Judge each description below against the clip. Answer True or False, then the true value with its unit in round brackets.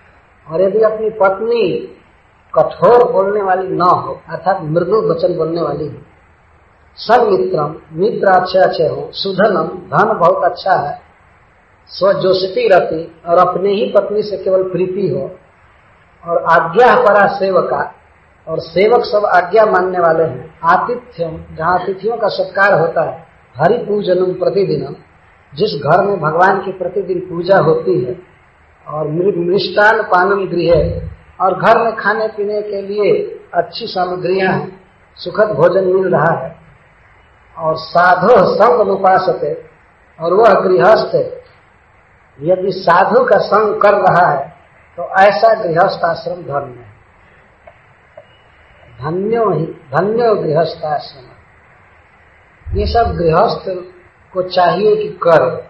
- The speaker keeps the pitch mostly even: False (3.6 semitones)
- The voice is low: False (185 Hz)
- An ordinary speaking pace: False (125 wpm)